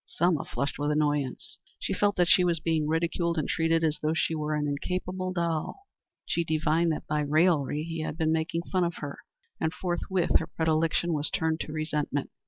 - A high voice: No, medium, 160 Hz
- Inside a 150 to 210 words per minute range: Yes, average, 195 wpm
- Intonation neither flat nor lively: No, narrow, 1.9 semitones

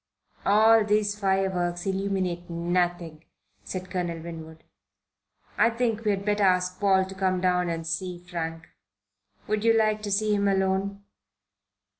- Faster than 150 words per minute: No, average, 140 wpm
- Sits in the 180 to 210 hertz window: Yes, high, 190 Hz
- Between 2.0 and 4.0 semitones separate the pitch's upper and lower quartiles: Yes, average, 2.7 semitones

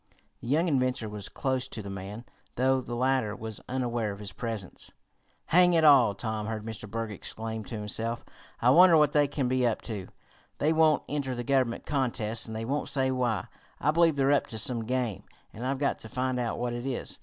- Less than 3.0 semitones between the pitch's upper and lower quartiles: No, average, 3.4 semitones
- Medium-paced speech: No, fast, 210 wpm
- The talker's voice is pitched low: Yes, low, 125 Hz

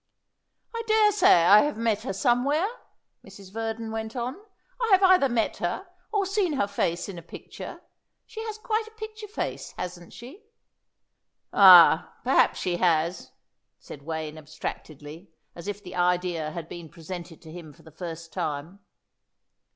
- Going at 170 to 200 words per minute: No, average, 155 wpm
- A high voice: Yes, high, 195 Hz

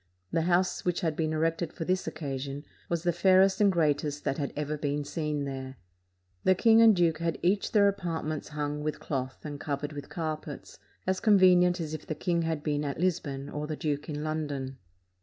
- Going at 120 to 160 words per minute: No, average, 195 wpm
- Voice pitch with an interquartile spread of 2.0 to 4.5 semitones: Yes, average, 3.2 semitones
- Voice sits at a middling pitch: Yes, medium, 155 Hz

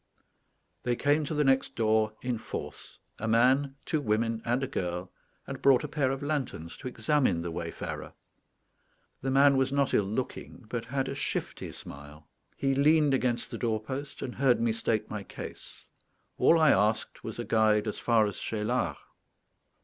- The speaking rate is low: No, average, 170 wpm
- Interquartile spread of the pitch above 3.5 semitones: Yes, average, 4.1 semitones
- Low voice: Yes, low, 120 Hz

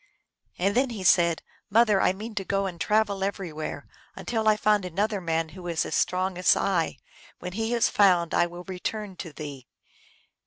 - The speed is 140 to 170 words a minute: No, average, 190 wpm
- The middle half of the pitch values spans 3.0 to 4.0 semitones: Yes, average, 3.3 semitones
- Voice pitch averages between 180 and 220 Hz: Yes, high, 190 Hz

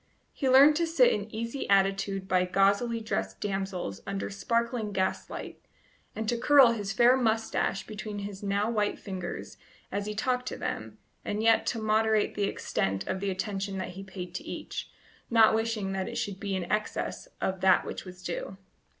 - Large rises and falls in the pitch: No, average, 2.8 semitones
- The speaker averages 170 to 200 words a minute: Yes, average, 180 wpm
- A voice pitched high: Yes, high, 205 Hz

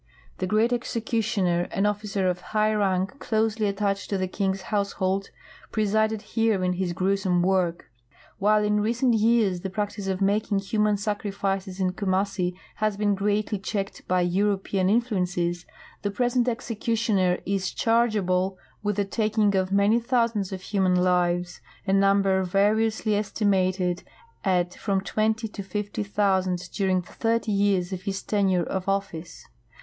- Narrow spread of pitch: Yes, narrow, 2.3 semitones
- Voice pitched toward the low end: No, high, 200 Hz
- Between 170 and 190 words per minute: No, average, 150 wpm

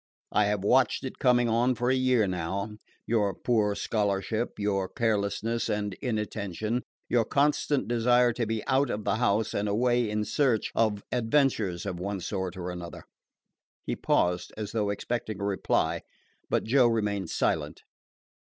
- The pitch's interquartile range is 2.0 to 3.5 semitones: Yes, average, 3.2 semitones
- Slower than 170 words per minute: Yes, average, 155 wpm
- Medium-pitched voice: No, low, 110 Hz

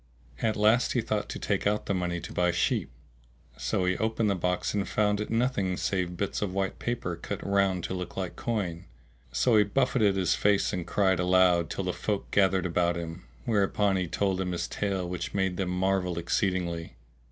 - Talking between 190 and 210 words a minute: Yes, average, 200 wpm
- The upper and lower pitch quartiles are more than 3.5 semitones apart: No, narrow, 2.5 semitones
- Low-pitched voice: Yes, very low, 95 Hz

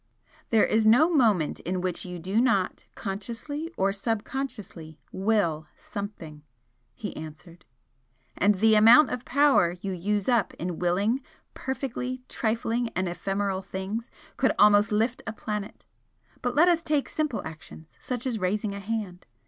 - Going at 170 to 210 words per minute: No, average, 145 wpm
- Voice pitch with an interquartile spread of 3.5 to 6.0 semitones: Yes, average, 4.5 semitones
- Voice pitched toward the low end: No, high, 210 Hz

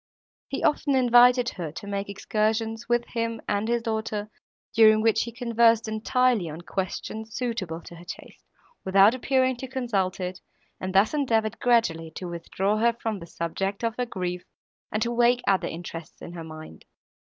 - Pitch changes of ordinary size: Yes, average, 4.1 semitones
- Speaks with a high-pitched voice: Yes, high, 220 Hz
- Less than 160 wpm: No, average, 170 wpm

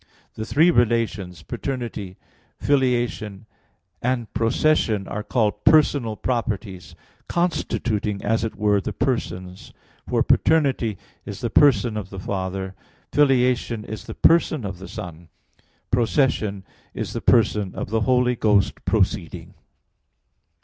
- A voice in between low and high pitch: No, low, 110 Hz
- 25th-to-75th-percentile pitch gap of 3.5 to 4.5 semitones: Yes, average, 4.1 semitones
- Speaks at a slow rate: Yes, slow, 120 wpm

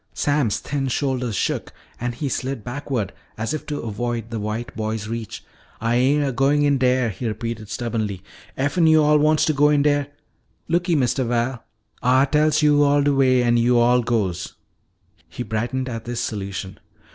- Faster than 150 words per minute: Yes, average, 170 wpm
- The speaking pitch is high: No, low, 125 Hz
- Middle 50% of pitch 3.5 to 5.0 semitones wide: Yes, average, 3.9 semitones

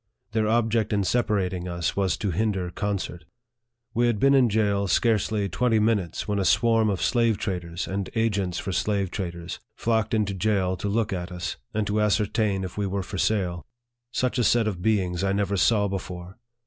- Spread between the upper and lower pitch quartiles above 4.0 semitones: No, average, 3.0 semitones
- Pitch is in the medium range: No, low, 100 Hz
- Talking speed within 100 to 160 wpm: No, average, 185 wpm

